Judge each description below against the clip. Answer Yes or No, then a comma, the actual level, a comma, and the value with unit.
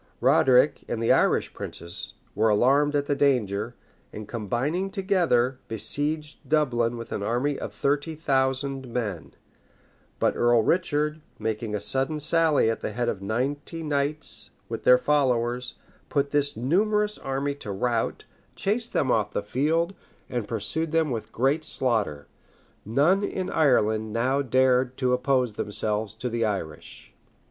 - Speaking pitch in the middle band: No, low, 130 Hz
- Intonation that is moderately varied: Yes, average, 4.7 semitones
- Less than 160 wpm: Yes, average, 145 wpm